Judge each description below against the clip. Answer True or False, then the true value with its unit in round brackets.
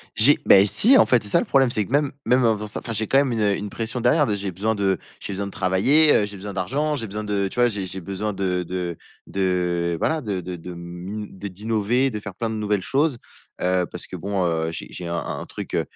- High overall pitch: False (100 Hz)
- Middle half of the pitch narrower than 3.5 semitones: False (3.9 semitones)